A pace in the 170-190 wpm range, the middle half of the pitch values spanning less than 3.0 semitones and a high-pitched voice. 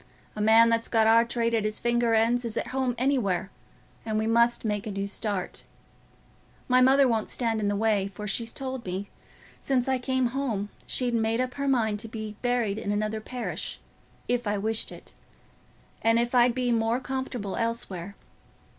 Yes: average, 185 wpm; narrow, 2.5 semitones; high, 230 Hz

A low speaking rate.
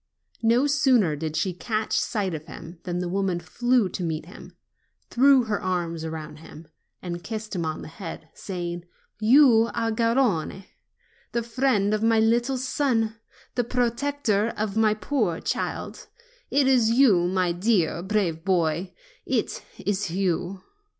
No: average, 150 wpm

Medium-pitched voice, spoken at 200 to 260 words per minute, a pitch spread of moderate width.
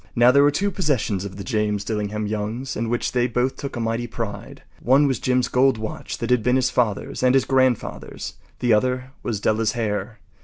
No: low, 120 Hz; fast, 205 wpm; average, 3.1 semitones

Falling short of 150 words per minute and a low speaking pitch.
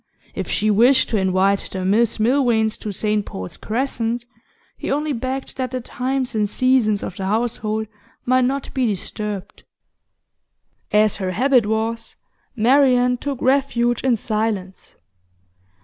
No: slow, 135 wpm; high, 230 Hz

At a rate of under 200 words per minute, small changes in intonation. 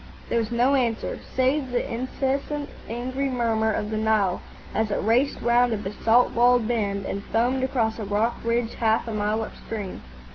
Yes: average, 175 wpm; narrow, 2.3 semitones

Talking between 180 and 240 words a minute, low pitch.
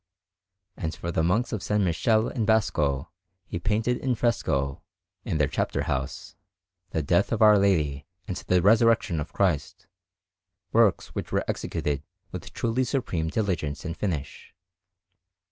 No: average, 145 wpm; very low, 95 Hz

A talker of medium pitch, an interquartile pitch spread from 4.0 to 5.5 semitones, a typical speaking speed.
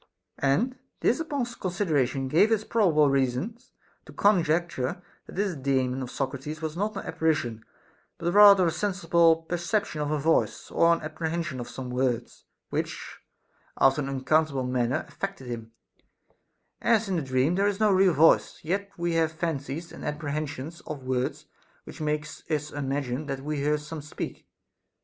Yes: medium, 155 Hz; average, 4.5 semitones; average, 160 wpm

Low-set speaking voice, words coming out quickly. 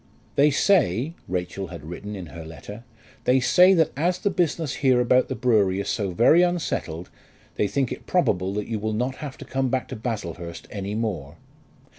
No: low, 115 Hz; average, 190 wpm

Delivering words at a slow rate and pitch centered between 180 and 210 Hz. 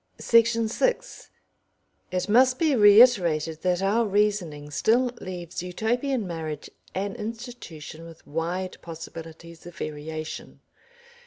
Yes: slow, 105 wpm; medium, 185 Hz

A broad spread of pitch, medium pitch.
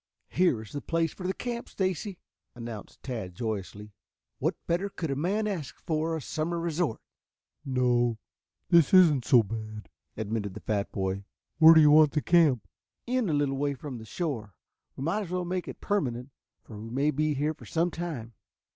Yes: wide, 6.9 semitones; medium, 145 Hz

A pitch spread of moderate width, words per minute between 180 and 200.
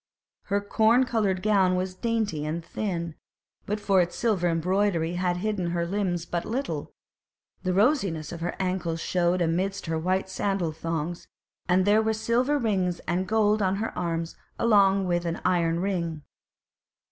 No: average, 3.3 semitones; average, 160 wpm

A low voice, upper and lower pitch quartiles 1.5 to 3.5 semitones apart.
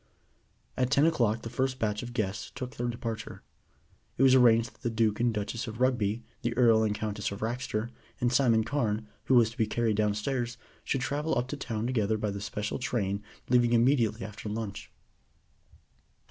Yes: low, 115 Hz; narrow, 2.5 semitones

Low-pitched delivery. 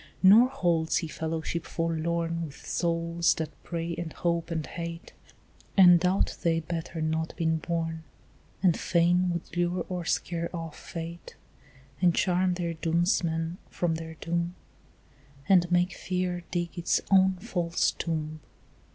No: medium, 170 Hz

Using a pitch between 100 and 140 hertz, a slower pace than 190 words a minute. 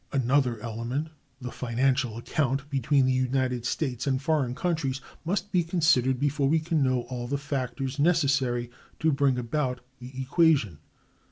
Yes: low, 135 Hz; average, 150 wpm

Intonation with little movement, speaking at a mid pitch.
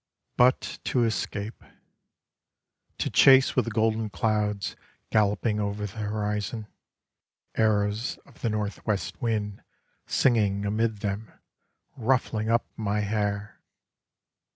No: narrow, 1.6 semitones; low, 105 Hz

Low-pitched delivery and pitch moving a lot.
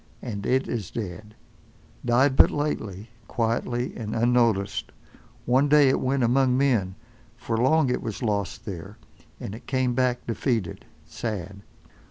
No: low, 120 Hz; average, 3.8 semitones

